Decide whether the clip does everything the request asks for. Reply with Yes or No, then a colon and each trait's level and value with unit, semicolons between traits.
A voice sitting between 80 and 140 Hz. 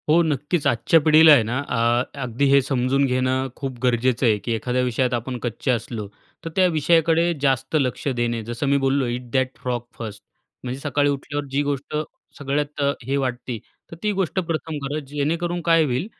Yes: low, 135 Hz